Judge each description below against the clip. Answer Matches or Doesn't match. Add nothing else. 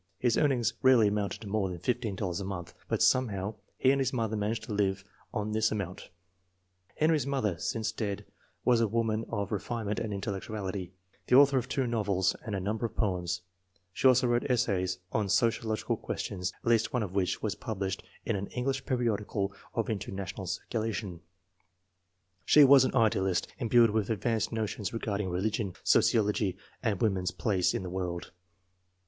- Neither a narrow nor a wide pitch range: Matches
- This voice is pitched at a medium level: Doesn't match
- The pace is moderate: Matches